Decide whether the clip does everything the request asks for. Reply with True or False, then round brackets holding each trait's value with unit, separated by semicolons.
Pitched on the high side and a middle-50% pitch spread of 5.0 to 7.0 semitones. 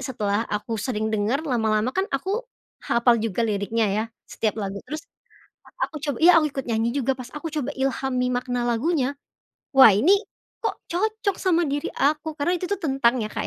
True (260 Hz; 5.3 semitones)